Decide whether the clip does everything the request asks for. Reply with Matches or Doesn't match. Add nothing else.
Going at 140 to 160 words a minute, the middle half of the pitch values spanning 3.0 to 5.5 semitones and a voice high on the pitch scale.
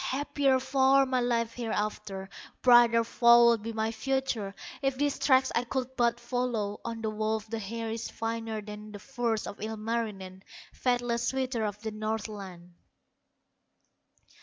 Doesn't match